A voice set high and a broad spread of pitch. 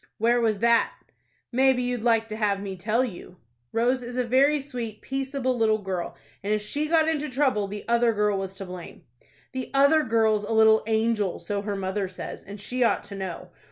No: high, 225 Hz; average, 3.7 semitones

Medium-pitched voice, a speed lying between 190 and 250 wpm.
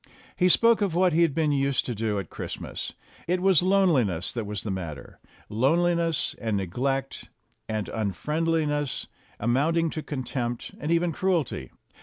No: medium, 145 Hz; average, 155 wpm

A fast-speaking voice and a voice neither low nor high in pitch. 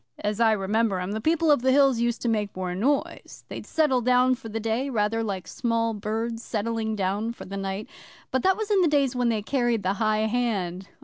No: fast, 225 wpm; high, 225 Hz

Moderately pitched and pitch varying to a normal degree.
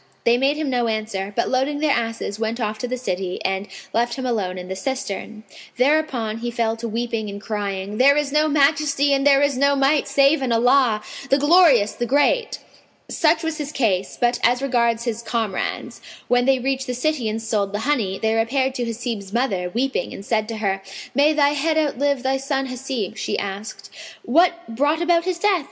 No: high, 245 Hz; average, 4.3 semitones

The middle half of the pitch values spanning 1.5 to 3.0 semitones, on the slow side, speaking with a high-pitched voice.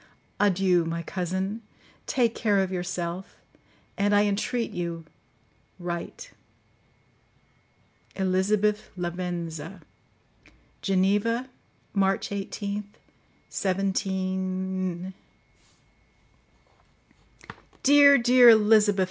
Yes: narrow, 2.4 semitones; slow, 65 wpm; high, 195 Hz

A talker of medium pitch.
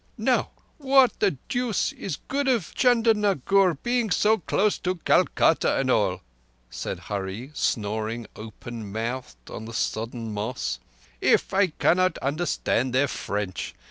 Yes: medium, 145 Hz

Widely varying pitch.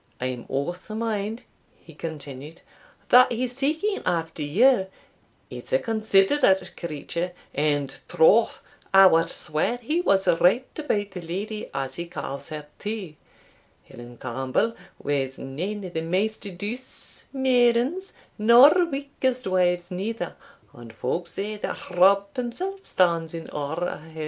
Yes: wide, 6.5 semitones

